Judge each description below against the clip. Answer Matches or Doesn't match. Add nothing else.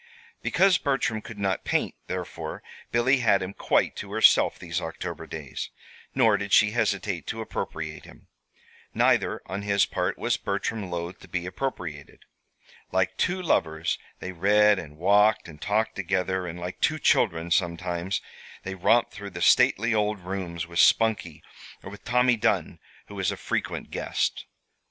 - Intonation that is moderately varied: Matches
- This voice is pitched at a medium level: Doesn't match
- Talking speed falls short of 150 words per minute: Doesn't match